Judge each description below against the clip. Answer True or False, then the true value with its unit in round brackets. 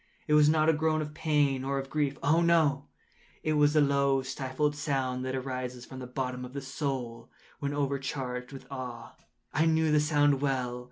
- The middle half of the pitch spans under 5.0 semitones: True (2.4 semitones)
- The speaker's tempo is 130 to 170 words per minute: False (180 wpm)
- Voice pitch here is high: False (140 Hz)